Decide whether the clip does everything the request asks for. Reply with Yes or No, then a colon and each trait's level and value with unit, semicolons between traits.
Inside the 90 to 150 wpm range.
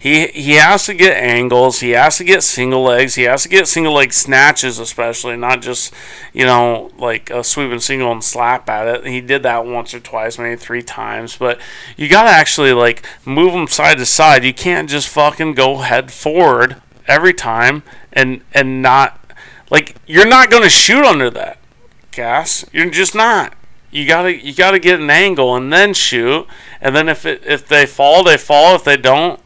No: average, 200 wpm